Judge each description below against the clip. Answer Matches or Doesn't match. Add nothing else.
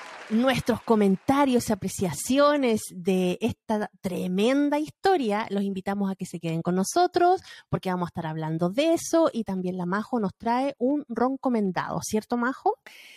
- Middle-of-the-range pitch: Doesn't match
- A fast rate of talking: Doesn't match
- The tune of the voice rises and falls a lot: Matches